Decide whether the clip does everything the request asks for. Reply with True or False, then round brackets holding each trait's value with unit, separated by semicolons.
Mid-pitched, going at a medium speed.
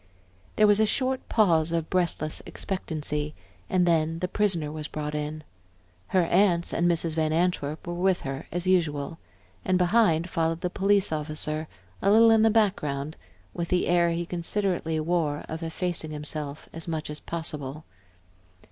True (165 Hz; 165 wpm)